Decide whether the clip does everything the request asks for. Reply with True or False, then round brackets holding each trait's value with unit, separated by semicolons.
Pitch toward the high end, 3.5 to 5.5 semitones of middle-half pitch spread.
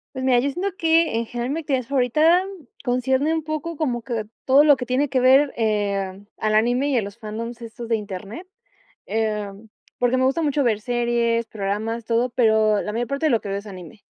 True (240 Hz; 4.1 semitones)